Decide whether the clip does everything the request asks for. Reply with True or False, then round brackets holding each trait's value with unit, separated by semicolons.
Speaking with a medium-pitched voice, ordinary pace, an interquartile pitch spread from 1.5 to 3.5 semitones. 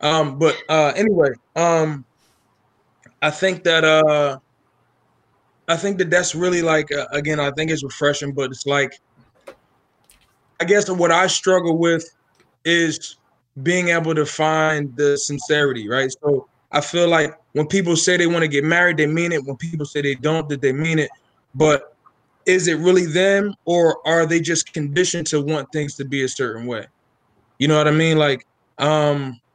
True (155 Hz; 175 wpm; 2.9 semitones)